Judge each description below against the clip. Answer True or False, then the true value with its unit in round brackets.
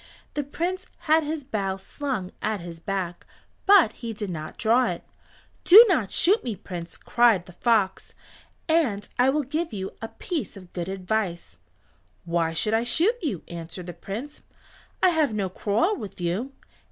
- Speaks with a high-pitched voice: True (220 Hz)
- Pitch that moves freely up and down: True (8.1 semitones)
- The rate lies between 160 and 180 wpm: True (165 wpm)